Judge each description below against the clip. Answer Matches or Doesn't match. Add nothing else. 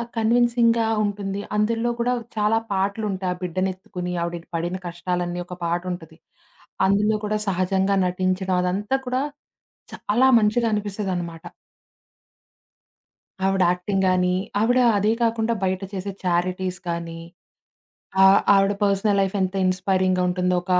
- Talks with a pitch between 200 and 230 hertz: Doesn't match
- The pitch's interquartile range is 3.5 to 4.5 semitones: Doesn't match